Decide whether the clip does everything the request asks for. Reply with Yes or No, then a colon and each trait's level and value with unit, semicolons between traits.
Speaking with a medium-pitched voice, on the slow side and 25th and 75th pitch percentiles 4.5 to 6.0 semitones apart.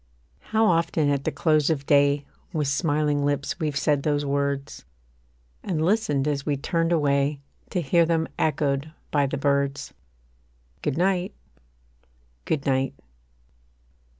No: medium, 145 Hz; slow, 130 wpm; narrow, 2.5 semitones